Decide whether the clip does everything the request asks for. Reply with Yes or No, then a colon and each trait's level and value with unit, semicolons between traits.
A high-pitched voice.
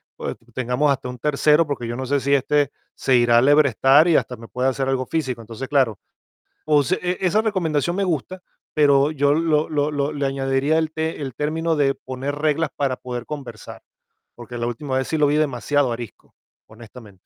No: medium, 140 Hz